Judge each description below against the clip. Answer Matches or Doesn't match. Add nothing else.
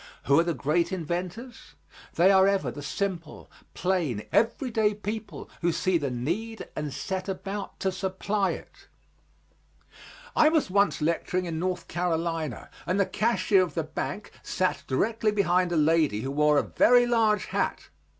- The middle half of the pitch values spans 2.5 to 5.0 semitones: Matches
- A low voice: Doesn't match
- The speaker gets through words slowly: Doesn't match